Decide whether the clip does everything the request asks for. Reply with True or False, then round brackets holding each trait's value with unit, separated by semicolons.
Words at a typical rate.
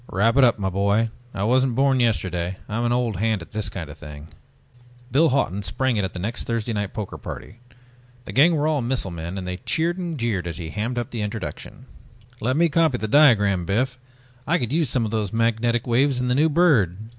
False (225 wpm)